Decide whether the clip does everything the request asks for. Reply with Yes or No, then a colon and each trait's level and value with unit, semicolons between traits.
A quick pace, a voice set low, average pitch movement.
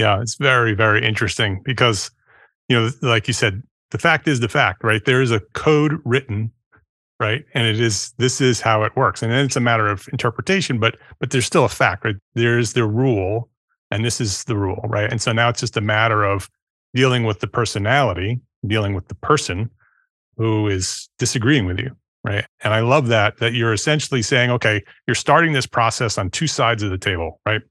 Yes: fast, 210 wpm; low, 115 Hz; average, 3.0 semitones